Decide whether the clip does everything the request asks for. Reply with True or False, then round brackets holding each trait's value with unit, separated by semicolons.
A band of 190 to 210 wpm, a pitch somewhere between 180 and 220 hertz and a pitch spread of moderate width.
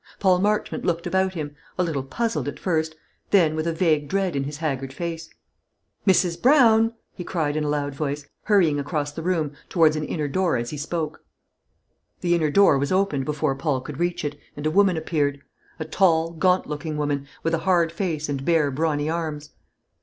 False (195 wpm; 160 Hz; 3.3 semitones)